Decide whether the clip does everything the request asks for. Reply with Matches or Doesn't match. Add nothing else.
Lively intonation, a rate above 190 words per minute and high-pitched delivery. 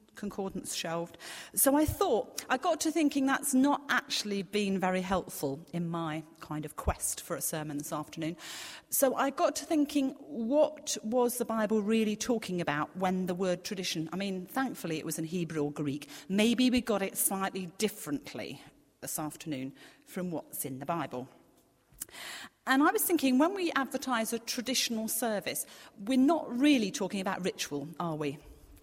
Doesn't match